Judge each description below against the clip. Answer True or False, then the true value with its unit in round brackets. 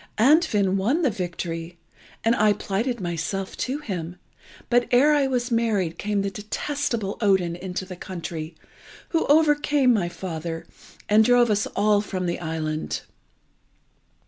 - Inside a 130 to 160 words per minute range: True (140 wpm)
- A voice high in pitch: True (205 Hz)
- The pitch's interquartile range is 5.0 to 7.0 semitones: True (5.6 semitones)